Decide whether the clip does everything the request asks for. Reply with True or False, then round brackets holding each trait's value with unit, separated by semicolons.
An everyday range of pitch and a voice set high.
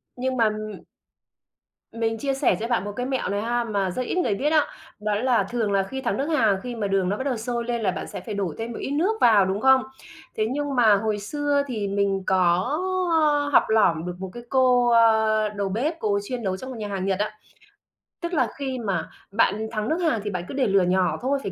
True (4.5 semitones; 225 Hz)